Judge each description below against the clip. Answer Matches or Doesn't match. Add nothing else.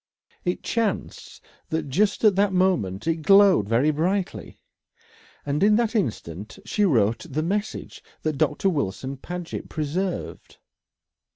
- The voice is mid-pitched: Matches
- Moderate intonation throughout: Doesn't match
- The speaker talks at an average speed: Doesn't match